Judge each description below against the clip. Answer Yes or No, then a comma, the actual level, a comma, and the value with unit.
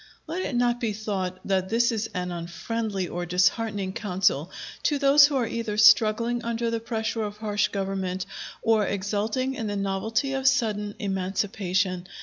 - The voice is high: Yes, high, 210 Hz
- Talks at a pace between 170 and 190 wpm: No, average, 160 wpm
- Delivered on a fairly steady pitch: No, average, 3.3 semitones